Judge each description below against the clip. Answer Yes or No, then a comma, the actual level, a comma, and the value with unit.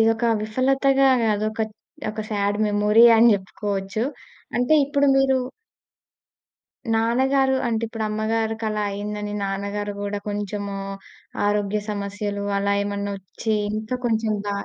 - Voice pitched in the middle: No, high, 215 Hz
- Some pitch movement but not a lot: No, narrow, 1.9 semitones